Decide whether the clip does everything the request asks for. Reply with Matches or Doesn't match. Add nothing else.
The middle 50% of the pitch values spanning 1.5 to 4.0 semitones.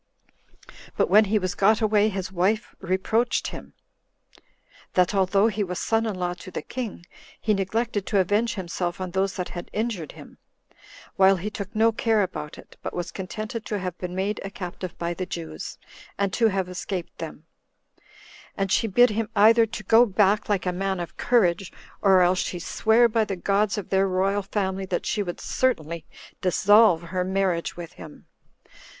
Matches